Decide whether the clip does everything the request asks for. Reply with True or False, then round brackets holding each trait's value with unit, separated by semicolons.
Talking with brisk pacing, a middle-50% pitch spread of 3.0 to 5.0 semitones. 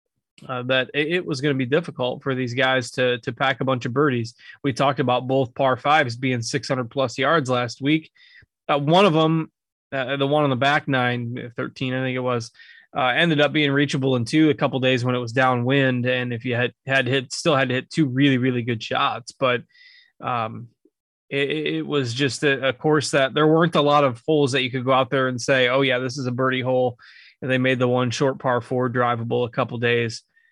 False (230 wpm; 2.4 semitones)